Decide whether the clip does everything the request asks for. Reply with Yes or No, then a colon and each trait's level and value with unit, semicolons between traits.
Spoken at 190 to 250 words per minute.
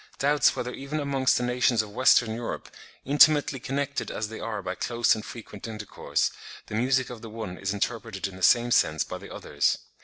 Yes: average, 195 wpm